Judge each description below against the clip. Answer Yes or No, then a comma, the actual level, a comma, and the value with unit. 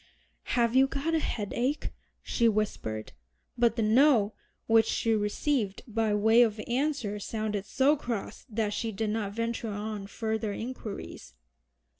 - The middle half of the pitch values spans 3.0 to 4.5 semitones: No, narrow, 2.6 semitones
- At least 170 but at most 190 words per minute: No, average, 140 wpm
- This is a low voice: No, high, 225 Hz